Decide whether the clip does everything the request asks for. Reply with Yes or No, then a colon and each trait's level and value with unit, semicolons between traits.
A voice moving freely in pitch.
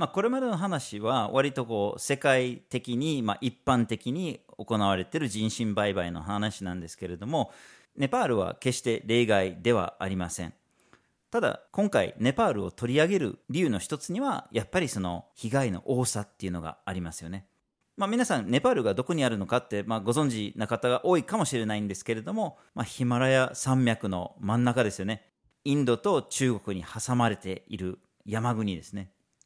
No: average, 4.8 semitones